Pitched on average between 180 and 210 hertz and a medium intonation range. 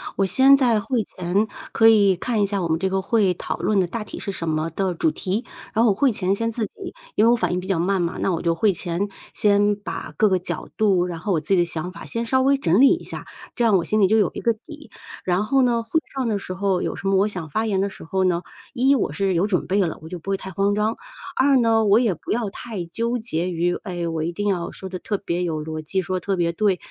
Yes: high, 195 Hz; average, 4.0 semitones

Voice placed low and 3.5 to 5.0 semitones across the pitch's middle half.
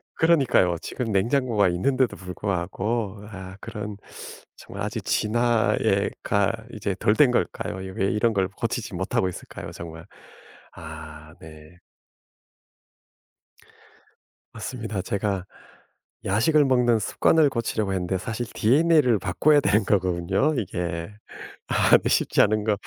Yes: low, 105 Hz; average, 4.3 semitones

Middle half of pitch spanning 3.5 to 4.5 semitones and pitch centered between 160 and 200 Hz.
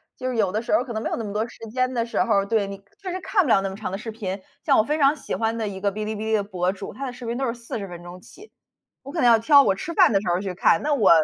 No: average, 4.2 semitones; high, 220 Hz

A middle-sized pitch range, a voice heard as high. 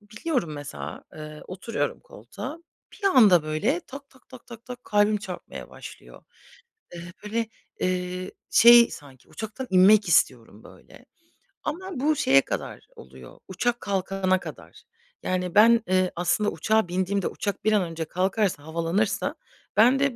Yes: average, 4.9 semitones; high, 200 Hz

